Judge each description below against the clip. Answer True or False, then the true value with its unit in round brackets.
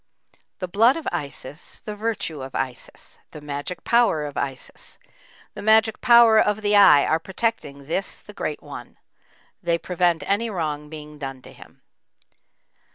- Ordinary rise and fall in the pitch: False (6.7 semitones)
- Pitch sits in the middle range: True (175 Hz)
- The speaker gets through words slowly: False (155 wpm)